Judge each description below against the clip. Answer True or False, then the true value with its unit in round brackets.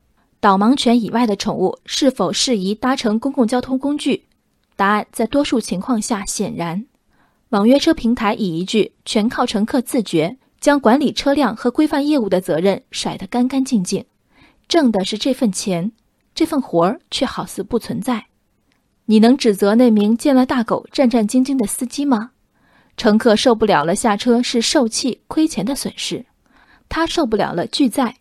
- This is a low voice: False (235 Hz)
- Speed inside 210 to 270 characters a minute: True (255 characters per minute)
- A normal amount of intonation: True (4.3 semitones)